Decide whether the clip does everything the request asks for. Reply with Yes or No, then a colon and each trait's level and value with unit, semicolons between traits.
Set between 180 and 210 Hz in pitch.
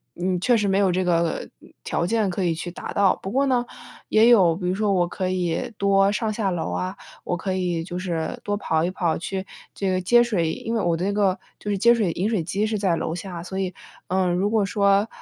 Yes: high, 190 Hz